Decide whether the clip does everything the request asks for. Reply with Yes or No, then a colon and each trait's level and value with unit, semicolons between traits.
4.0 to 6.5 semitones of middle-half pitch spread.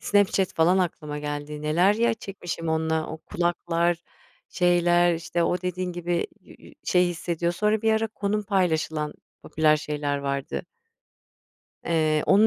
No: average, 2.8 semitones